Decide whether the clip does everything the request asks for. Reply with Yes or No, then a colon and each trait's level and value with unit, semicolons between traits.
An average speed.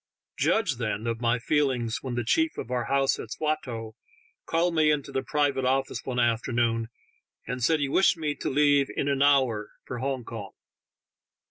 Yes: average, 175 wpm